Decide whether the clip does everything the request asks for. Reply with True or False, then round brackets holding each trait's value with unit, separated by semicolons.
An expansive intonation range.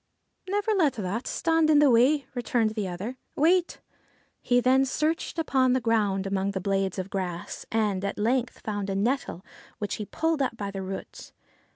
True (5.8 semitones)